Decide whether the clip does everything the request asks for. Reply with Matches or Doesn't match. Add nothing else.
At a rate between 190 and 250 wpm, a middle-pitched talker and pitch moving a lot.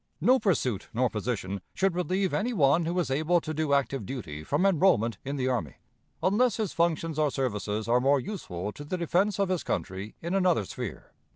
Matches